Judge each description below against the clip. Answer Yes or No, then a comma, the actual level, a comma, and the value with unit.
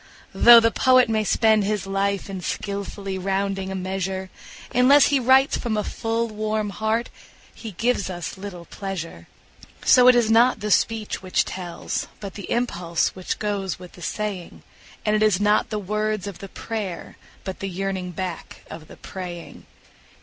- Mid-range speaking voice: No, high, 200 Hz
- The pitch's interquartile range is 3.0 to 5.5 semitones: No, narrow, 2.6 semitones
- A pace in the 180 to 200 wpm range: No, average, 170 wpm